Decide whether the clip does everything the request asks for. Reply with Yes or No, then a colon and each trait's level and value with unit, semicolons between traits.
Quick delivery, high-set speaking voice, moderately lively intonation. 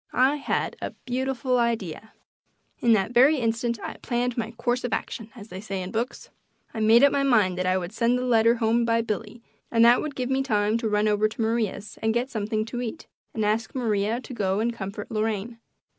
No: fast, 220 wpm; high, 230 Hz; narrow, 2.3 semitones